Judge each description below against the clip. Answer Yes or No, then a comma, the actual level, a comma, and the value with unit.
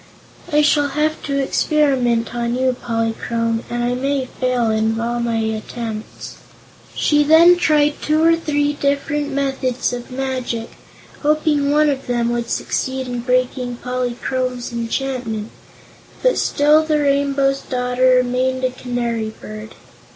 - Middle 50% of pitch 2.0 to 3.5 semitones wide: Yes, average, 3.2 semitones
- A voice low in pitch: No, very high, 255 Hz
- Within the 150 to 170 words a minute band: No, slow, 135 wpm